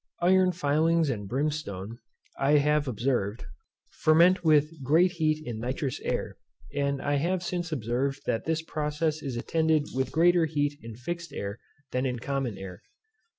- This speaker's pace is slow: No, average, 150 wpm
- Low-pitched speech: No, medium, 145 Hz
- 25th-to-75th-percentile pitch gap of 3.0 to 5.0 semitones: Yes, average, 4.1 semitones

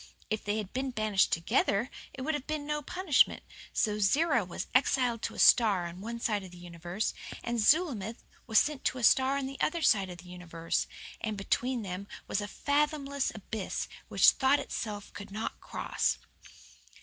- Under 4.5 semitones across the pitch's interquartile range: No, wide, 5.6 semitones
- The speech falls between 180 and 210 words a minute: Yes, average, 185 wpm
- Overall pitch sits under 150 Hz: No, high, 225 Hz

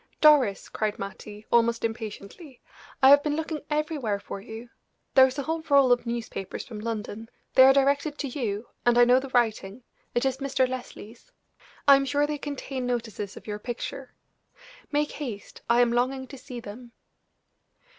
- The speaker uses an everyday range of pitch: Yes, average, 3.7 semitones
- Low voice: No, very high, 250 Hz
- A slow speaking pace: No, average, 175 wpm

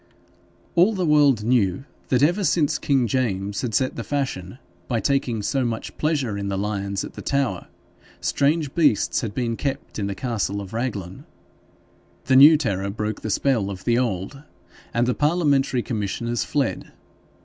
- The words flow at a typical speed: Yes, average, 165 wpm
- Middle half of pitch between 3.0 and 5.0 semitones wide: No, wide, 5.5 semitones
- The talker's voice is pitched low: Yes, low, 120 Hz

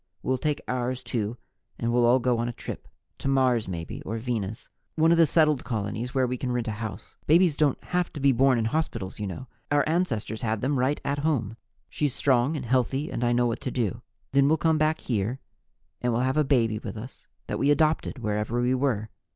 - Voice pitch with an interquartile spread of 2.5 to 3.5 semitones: No, average, 4.0 semitones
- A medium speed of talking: No, fast, 225 wpm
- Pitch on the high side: No, low, 125 Hz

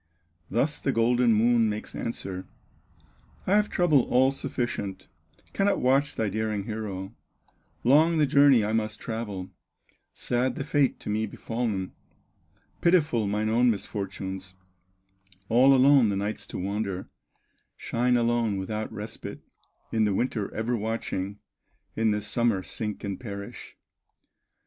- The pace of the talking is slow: Yes, slow, 130 wpm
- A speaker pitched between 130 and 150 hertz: No, low, 110 Hz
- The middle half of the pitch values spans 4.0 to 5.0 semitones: No, average, 3.4 semitones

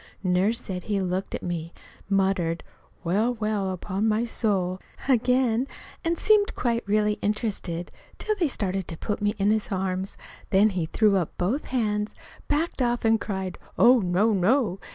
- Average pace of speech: Yes, average, 160 wpm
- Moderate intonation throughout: Yes, average, 3.7 semitones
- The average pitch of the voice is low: No, high, 205 Hz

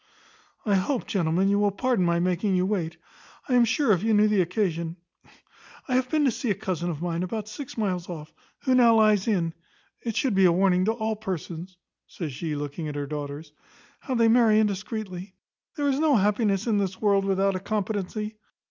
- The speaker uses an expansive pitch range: No, average, 3.9 semitones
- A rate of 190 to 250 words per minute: Yes, average, 200 wpm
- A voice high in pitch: Yes, high, 195 Hz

